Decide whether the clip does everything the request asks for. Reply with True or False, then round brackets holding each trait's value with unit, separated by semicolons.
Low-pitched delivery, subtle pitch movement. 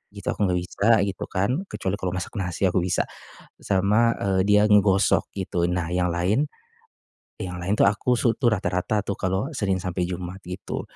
True (95 Hz; 2.2 semitones)